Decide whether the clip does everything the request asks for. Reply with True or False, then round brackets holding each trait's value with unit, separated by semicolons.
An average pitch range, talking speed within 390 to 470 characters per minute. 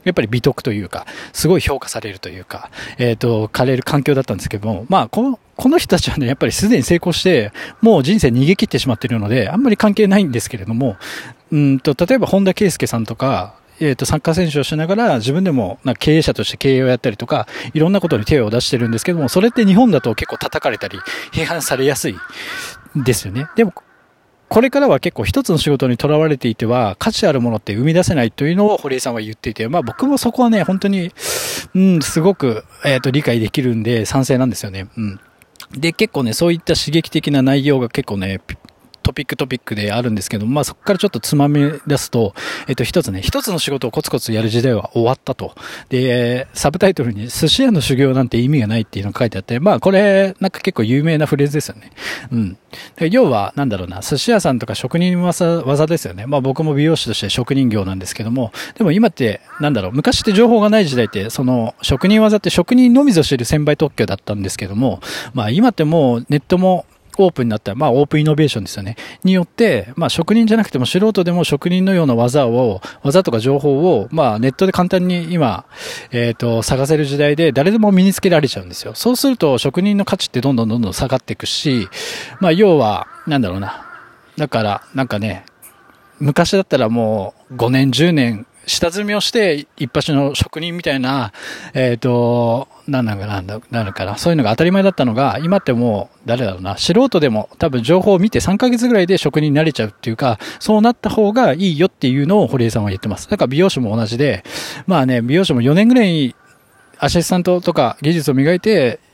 False (7.1 semitones; 440 characters per minute)